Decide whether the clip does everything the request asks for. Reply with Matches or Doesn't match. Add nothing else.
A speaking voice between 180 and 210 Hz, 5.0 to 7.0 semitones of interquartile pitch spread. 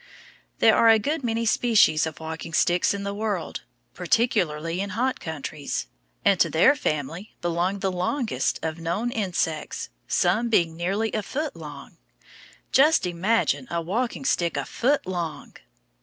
Matches